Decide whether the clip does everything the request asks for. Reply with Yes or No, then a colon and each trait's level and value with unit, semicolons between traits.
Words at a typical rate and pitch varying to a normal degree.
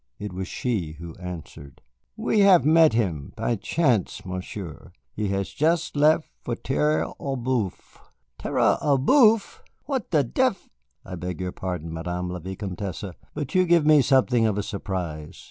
No: average, 160 wpm; wide, 8.8 semitones